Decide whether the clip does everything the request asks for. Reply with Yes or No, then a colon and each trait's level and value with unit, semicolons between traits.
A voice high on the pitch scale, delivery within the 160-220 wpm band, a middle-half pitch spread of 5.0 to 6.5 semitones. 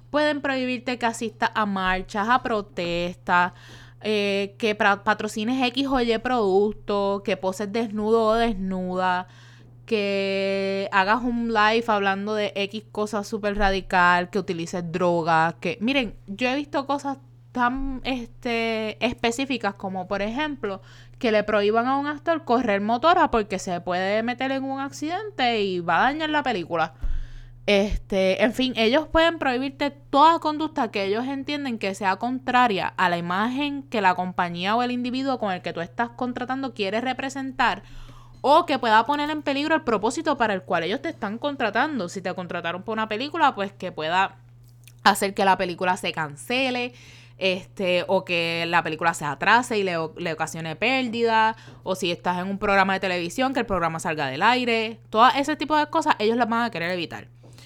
Yes: high, 210 Hz; average, 170 wpm; wide, 5.5 semitones